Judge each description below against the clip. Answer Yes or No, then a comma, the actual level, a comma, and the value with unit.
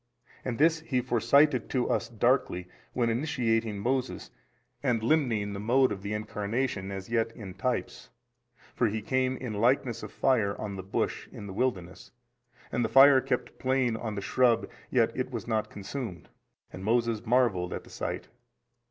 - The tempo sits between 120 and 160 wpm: No, average, 170 wpm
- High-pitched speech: No, low, 115 Hz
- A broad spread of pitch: No, average, 3.7 semitones